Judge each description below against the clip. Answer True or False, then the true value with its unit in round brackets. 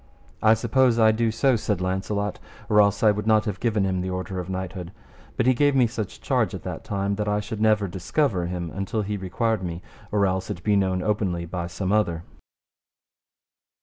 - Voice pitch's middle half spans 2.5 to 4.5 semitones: True (2.9 semitones)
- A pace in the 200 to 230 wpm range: True (205 wpm)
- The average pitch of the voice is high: False (100 Hz)